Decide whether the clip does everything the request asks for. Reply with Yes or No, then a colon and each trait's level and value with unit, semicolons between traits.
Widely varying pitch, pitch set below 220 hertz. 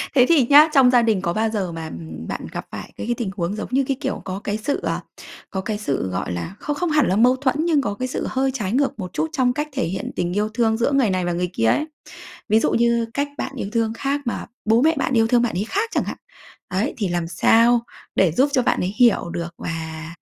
No: wide, 6.2 semitones; high, 225 Hz